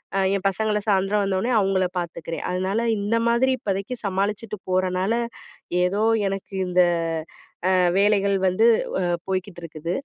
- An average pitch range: No, narrow, 2.1 semitones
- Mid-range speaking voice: No, high, 195 Hz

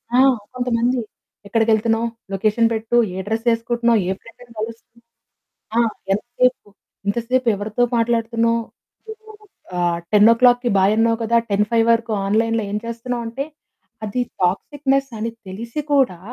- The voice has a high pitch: Yes, high, 230 Hz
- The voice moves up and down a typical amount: No, narrow, 1.7 semitones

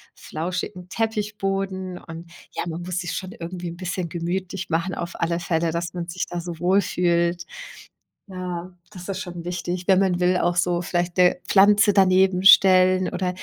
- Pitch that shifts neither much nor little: No, narrow, 1.5 semitones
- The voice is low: No, medium, 180 Hz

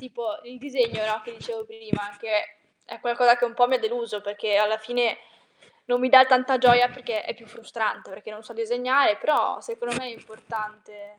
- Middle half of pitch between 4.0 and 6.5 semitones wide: No, average, 2.7 semitones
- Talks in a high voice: Yes, high, 240 Hz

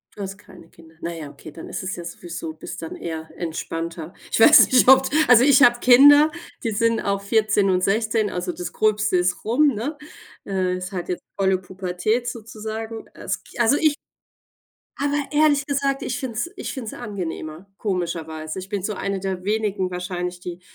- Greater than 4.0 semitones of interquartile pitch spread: Yes, average, 5.0 semitones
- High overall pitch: Yes, high, 200 Hz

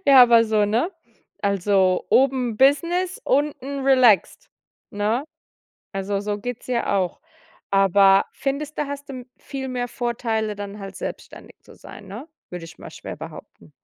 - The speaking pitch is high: Yes, high, 235 Hz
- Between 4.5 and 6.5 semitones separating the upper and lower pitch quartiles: Yes, average, 5.2 semitones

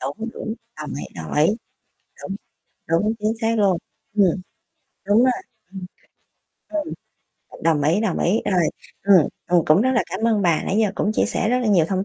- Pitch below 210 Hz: Yes, high, 195 Hz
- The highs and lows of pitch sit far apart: No, average, 4.7 semitones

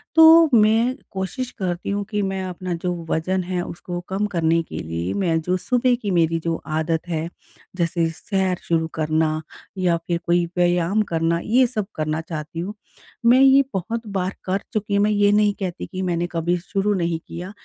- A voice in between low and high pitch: Yes, medium, 180 Hz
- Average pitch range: Yes, average, 3.5 semitones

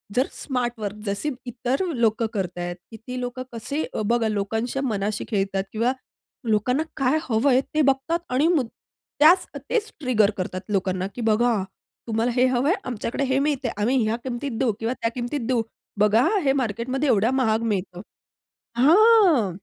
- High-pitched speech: Yes, high, 240 Hz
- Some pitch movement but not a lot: Yes, average, 3.8 semitones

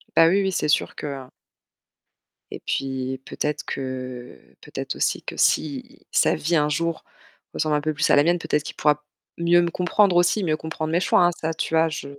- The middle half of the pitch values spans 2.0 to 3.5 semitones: Yes, average, 2.8 semitones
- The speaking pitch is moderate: Yes, medium, 155 Hz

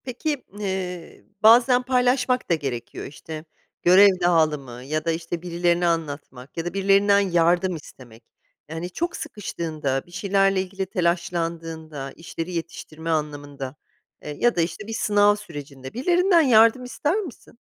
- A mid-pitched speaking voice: Yes, medium, 175 Hz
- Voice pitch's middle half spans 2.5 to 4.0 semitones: No, average, 4.8 semitones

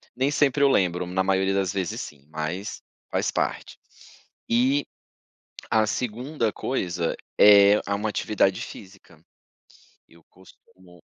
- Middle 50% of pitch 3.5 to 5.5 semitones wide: Yes, average, 4.2 semitones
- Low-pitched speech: Yes, low, 100 Hz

